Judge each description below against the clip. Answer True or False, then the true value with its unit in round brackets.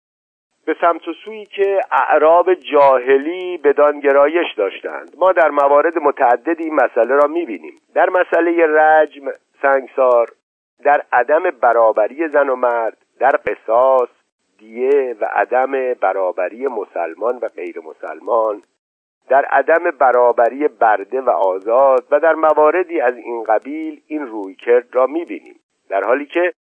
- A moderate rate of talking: True (125 wpm)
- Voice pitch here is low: False (160 Hz)